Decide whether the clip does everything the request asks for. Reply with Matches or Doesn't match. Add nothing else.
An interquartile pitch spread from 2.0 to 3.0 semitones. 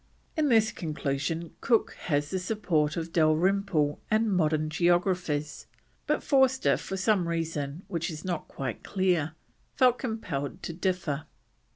Doesn't match